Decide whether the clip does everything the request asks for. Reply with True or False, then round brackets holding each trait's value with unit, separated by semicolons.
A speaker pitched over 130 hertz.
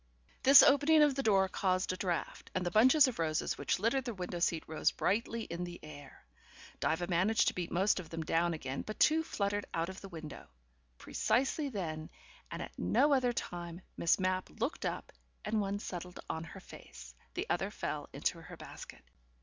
True (185 Hz)